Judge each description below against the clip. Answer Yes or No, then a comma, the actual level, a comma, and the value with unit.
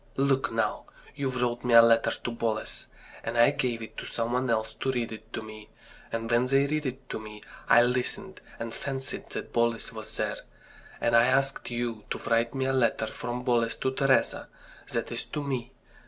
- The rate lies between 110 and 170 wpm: No, average, 200 wpm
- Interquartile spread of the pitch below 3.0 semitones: Yes, narrow, 2.4 semitones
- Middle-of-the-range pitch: No, low, 120 Hz